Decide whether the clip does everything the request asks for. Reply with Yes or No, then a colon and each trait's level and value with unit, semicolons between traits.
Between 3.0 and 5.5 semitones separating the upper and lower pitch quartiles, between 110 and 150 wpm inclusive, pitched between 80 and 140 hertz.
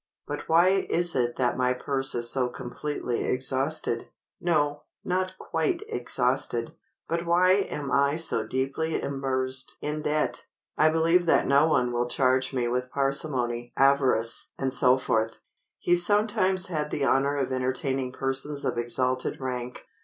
Yes: average, 3.7 semitones; average, 140 wpm; low, 135 Hz